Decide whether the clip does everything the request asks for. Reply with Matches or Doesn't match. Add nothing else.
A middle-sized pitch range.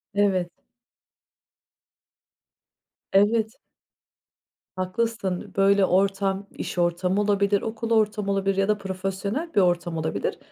Doesn't match